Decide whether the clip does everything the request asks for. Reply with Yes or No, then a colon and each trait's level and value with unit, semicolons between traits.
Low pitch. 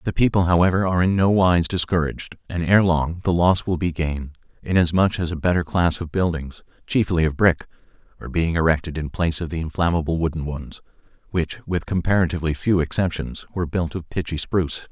Yes: very low, 85 Hz